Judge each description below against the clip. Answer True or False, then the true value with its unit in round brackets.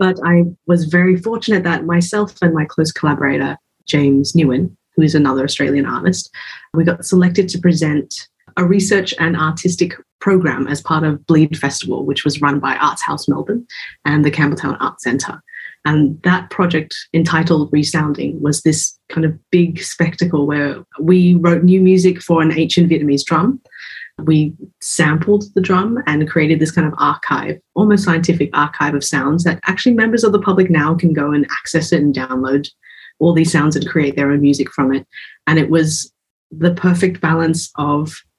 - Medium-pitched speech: True (160 Hz)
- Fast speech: False (175 wpm)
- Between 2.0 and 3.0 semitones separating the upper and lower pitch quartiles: False (3.4 semitones)